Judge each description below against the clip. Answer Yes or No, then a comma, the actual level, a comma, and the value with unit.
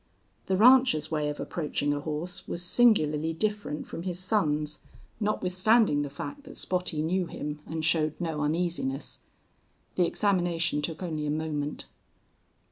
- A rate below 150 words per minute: Yes, average, 140 wpm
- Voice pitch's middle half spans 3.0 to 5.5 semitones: Yes, average, 3.6 semitones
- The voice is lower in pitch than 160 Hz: No, medium, 165 Hz